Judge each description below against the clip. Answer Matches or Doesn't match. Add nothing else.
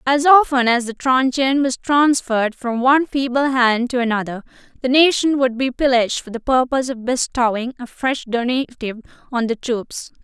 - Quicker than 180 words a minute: Doesn't match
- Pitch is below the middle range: Doesn't match